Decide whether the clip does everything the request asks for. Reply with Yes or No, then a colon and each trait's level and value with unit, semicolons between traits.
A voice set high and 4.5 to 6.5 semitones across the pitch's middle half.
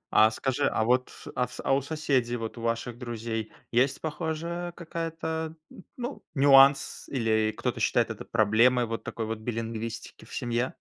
No: low, 125 Hz; average, 5.2 semitones